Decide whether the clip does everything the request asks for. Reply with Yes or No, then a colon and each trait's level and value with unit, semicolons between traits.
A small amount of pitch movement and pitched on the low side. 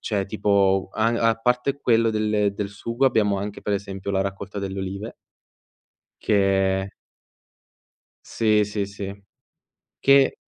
Yes: narrow, 2.0 semitones; low, 100 Hz